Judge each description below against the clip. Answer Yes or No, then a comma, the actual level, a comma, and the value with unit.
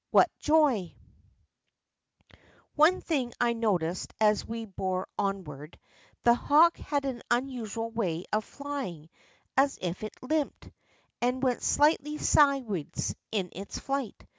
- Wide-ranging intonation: Yes, wide, 6.2 semitones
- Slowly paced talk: Yes, slow, 120 wpm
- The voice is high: Yes, high, 235 Hz